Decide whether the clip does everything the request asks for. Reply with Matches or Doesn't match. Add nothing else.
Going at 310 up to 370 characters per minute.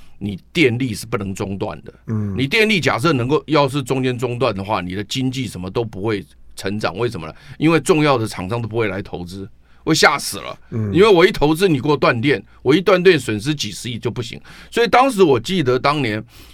Matches